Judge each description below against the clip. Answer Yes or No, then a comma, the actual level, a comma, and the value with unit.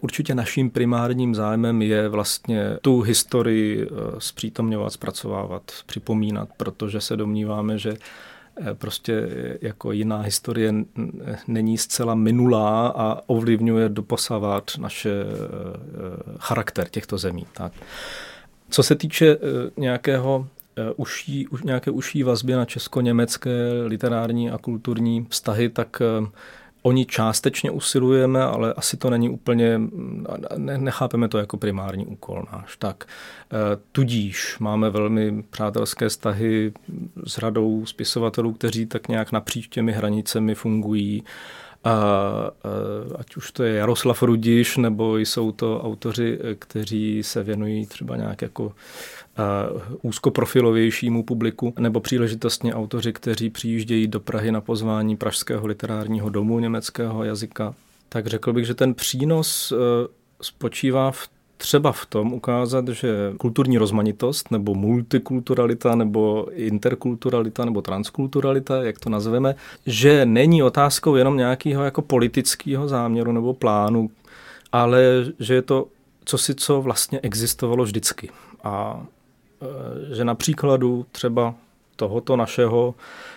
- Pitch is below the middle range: Yes, low, 115 Hz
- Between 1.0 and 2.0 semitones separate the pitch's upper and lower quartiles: No, narrow, 2.5 semitones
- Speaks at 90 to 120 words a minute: Yes, slow, 115 wpm